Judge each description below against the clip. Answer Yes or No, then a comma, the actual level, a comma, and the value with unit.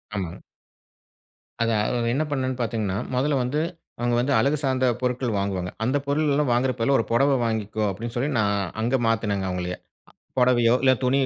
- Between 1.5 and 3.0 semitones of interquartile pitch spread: No, average, 3.5 semitones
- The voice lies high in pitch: No, low, 120 Hz